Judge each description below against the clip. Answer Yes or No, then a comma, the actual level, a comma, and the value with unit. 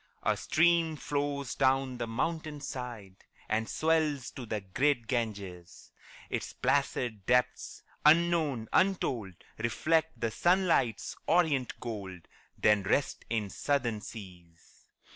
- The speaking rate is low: Yes, slow, 110 wpm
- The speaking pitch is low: Yes, low, 125 Hz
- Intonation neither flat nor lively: No, wide, 5.9 semitones